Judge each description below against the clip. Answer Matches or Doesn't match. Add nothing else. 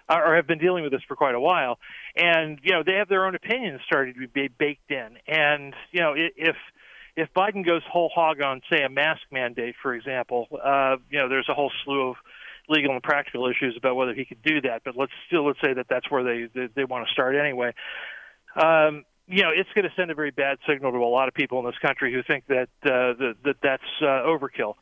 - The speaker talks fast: Matches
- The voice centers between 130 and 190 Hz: Matches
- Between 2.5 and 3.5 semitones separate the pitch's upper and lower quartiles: Doesn't match